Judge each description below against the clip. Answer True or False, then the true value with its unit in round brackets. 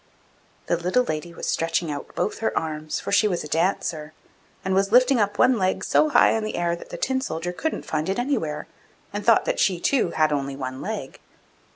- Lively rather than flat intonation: True (5.7 semitones)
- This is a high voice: False (175 Hz)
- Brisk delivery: True (215 wpm)